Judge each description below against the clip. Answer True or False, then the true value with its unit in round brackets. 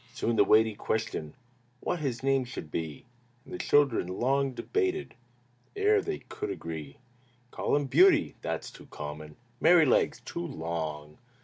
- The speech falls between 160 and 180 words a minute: False (145 wpm)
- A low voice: True (115 Hz)